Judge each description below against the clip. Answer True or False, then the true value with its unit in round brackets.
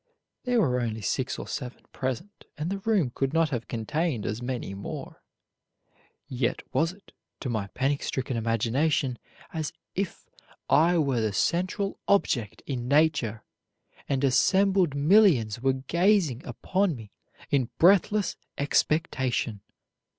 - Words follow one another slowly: True (130 wpm)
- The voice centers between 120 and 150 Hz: True (140 Hz)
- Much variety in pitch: True (6.3 semitones)